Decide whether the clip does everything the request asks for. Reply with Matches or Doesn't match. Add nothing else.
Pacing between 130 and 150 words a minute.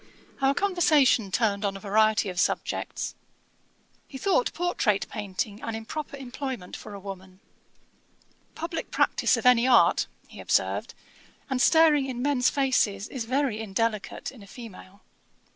Matches